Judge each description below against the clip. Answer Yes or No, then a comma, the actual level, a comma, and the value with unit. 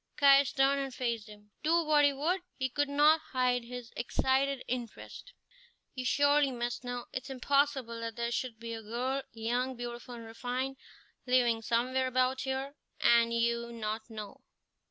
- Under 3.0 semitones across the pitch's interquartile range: Yes, narrow, 2.6 semitones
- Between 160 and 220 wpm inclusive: Yes, average, 165 wpm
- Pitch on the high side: Yes, very high, 250 Hz